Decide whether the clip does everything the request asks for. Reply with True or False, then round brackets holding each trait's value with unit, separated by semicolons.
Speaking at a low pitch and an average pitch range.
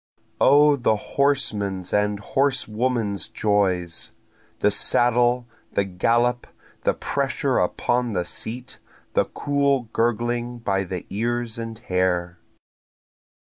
True (115 Hz; 3.7 semitones)